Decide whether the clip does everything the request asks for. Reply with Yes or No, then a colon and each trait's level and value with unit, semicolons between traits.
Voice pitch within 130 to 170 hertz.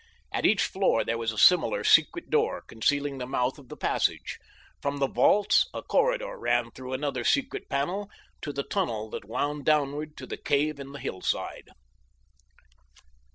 Yes: medium, 140 Hz